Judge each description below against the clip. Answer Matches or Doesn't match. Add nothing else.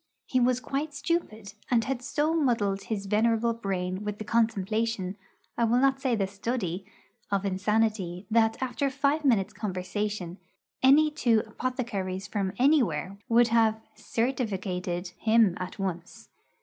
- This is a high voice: Matches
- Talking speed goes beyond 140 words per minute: Doesn't match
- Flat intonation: Doesn't match